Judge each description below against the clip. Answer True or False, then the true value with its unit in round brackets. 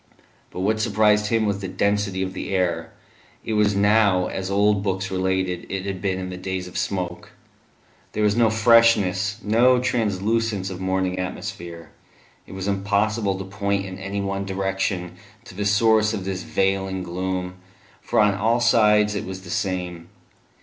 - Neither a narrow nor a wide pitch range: False (2.1 semitones)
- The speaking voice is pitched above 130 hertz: False (95 Hz)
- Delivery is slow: False (170 wpm)